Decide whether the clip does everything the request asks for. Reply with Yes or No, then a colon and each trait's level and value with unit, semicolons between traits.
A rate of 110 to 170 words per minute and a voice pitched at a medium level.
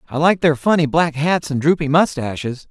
No: average, 200 wpm; medium, 150 Hz